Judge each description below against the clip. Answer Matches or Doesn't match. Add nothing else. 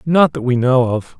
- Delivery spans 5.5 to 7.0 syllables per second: Doesn't match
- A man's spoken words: Matches